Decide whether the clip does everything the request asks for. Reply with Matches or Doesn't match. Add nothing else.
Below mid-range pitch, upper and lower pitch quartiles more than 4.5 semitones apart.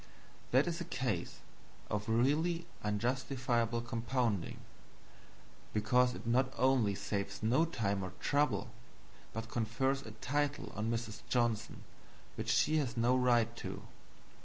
Doesn't match